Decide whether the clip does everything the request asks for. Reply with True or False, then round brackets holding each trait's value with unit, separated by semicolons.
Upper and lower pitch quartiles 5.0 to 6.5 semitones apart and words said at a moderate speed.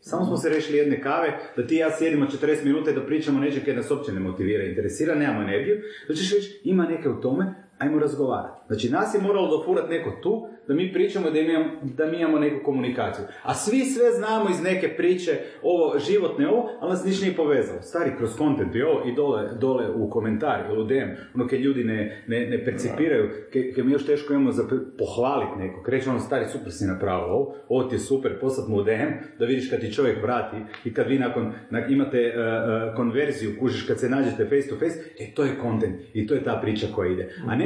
False (5.5 semitones; 225 wpm)